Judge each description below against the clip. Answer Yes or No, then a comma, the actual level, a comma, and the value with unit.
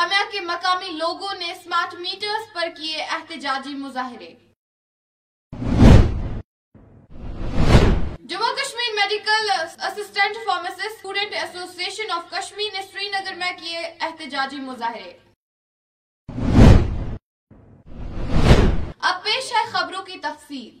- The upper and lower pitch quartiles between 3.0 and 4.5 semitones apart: Yes, average, 3.5 semitones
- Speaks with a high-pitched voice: Yes, very high, 365 Hz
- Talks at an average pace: No, slow, 95 wpm